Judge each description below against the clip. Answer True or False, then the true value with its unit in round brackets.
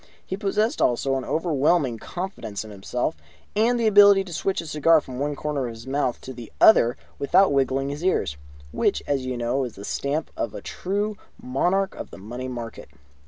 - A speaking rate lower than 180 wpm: False (195 wpm)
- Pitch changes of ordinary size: False (7.0 semitones)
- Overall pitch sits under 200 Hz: True (140 Hz)